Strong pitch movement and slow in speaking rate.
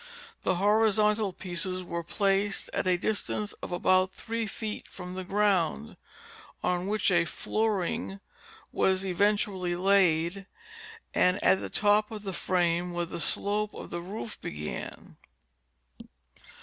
No: average, 2.9 semitones; slow, 130 wpm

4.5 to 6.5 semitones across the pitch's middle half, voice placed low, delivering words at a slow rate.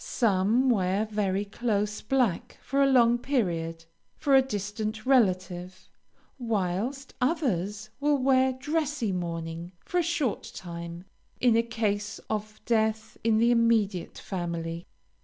No: average, 5.2 semitones; high, 215 Hz; slow, 125 wpm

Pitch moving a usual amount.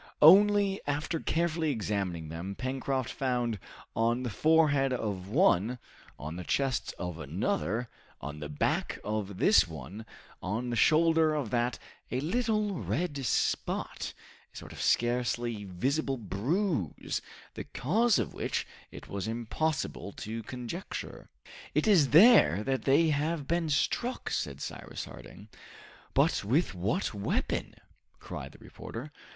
No: wide, 7.5 semitones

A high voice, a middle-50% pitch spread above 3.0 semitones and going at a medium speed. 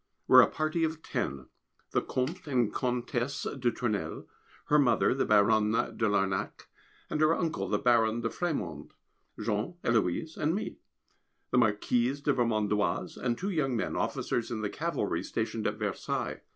No: low, 120 Hz; wide, 5.5 semitones; average, 160 wpm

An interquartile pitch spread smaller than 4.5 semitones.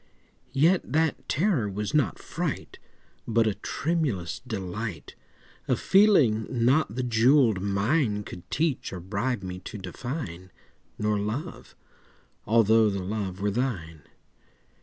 No: average, 5.3 semitones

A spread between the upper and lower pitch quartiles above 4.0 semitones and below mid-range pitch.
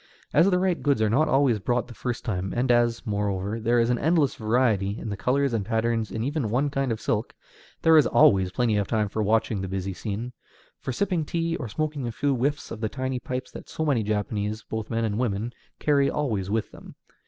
Yes: average, 4.4 semitones; low, 120 Hz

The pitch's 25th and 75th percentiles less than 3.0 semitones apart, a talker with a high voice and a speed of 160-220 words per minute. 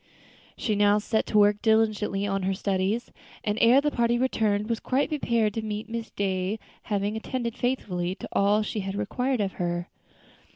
Yes: narrow, 2.6 semitones; high, 210 Hz; average, 175 wpm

